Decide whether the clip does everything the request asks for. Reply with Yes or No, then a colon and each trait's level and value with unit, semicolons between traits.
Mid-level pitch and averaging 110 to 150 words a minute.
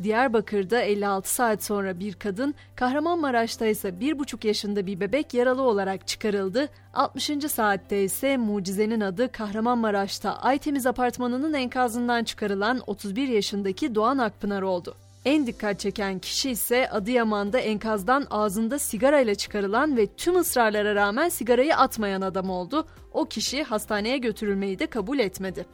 No: high, 220 Hz; average, 130 wpm